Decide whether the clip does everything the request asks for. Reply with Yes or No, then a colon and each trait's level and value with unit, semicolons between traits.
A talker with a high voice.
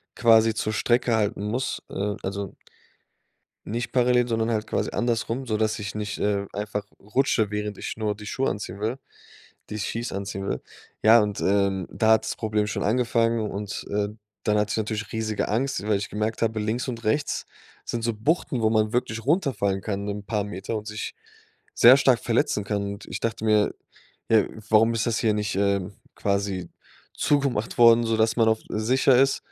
No: low, 110 Hz